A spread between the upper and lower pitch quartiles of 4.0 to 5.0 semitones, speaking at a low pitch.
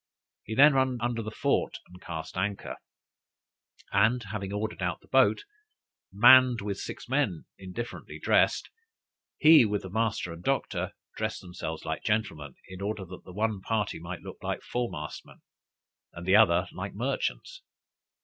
Yes: average, 4.3 semitones; low, 105 Hz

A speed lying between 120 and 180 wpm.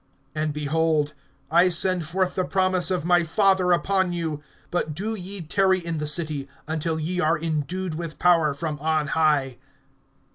Yes: average, 160 wpm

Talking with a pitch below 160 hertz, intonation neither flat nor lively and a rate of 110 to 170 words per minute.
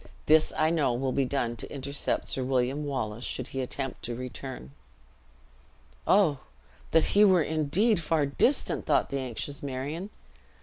Yes: medium, 140 Hz; average, 3.5 semitones; average, 155 wpm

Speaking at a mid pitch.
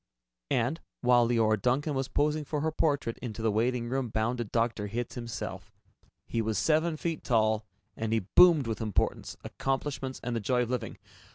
No: low, 120 Hz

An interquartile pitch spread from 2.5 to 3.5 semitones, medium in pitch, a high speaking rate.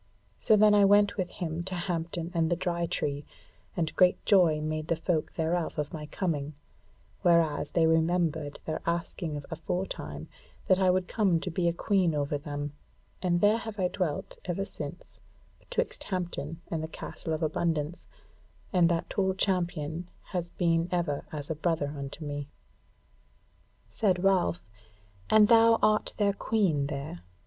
No: average, 3.1 semitones; medium, 170 Hz; average, 160 wpm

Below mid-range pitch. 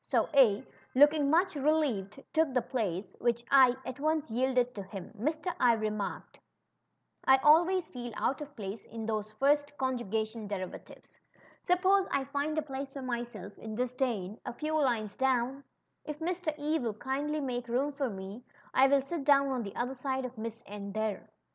No: very high, 260 Hz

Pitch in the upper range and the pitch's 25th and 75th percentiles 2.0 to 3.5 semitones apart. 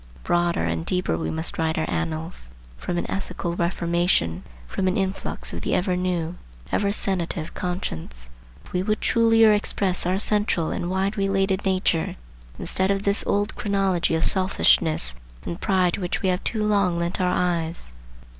No: medium, 180 Hz; average, 3.1 semitones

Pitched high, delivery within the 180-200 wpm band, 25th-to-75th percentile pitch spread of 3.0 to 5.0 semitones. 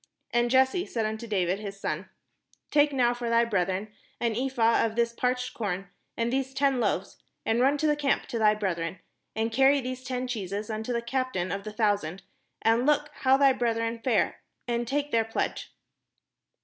Yes: high, 235 Hz; average, 185 wpm; average, 3.4 semitones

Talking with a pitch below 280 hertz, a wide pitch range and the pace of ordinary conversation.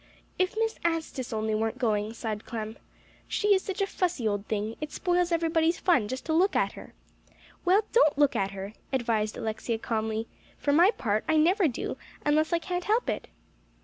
No: very high, 285 Hz; wide, 8.3 semitones; average, 185 wpm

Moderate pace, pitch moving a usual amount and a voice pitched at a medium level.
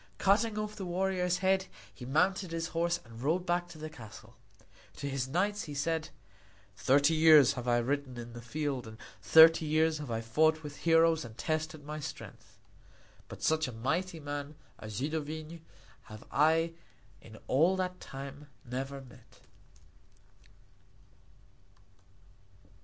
Yes: average, 145 wpm; average, 4.0 semitones; medium, 155 Hz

